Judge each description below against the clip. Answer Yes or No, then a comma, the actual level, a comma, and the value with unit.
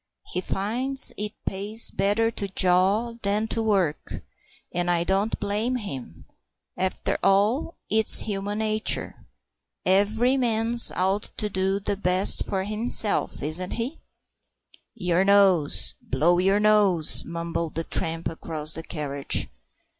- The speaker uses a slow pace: Yes, slow, 125 wpm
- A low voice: No, high, 195 Hz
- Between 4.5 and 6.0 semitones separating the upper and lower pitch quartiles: No, average, 3.4 semitones